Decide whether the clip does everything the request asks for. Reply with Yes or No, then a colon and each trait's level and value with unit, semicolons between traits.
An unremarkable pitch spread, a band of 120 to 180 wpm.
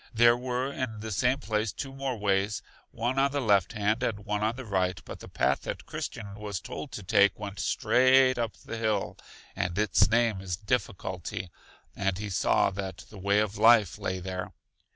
No: average, 3.4 semitones; average, 195 wpm